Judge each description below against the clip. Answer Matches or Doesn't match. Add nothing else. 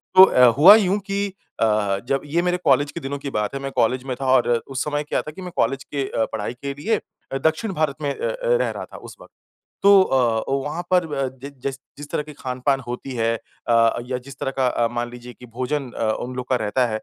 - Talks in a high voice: Doesn't match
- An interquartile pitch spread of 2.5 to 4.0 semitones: Matches